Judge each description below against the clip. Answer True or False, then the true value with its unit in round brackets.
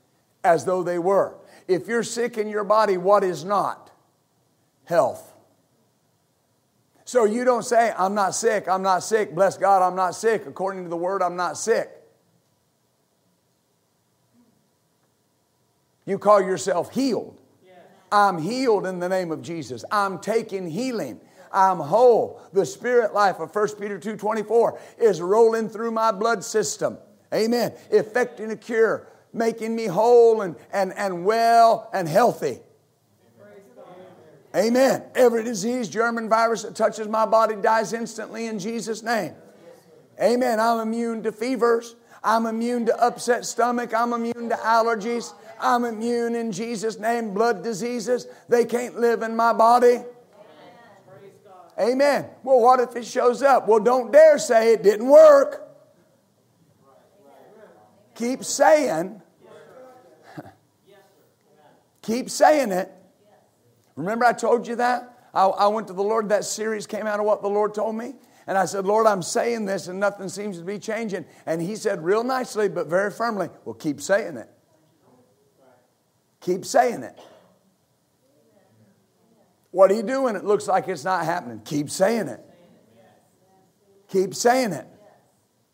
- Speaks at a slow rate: False (145 wpm)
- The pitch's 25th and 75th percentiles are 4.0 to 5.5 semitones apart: False (3.4 semitones)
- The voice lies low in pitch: False (220 Hz)